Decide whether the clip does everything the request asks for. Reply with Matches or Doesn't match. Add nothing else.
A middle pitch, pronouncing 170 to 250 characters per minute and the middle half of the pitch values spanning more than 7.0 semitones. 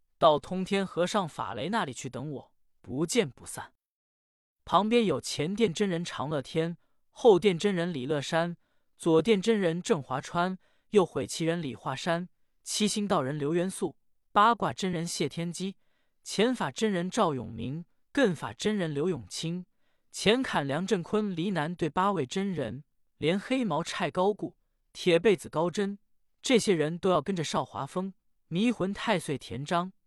Doesn't match